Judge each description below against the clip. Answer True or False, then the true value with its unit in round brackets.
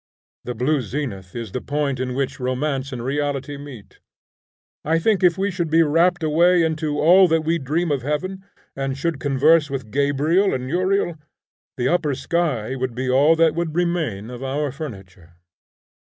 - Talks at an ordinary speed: True (170 wpm)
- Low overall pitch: False (145 Hz)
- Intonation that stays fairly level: False (4.3 semitones)